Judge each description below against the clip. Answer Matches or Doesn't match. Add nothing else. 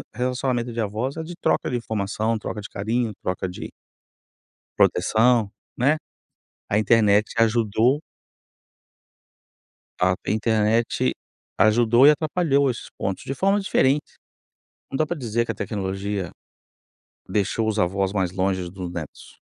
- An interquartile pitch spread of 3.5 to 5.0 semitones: Matches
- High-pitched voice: Doesn't match